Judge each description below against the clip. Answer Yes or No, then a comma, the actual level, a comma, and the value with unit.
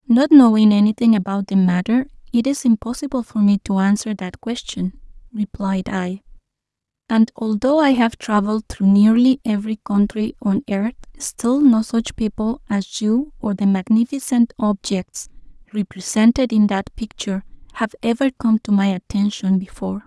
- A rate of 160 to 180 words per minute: No, average, 145 wpm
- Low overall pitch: No, high, 220 Hz